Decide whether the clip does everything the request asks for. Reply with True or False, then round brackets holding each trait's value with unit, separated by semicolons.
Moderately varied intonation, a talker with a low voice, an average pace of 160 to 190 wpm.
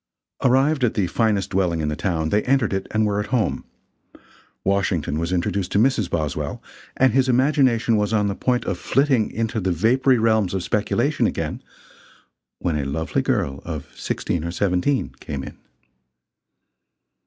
False (5.9 semitones; 105 Hz; 165 wpm)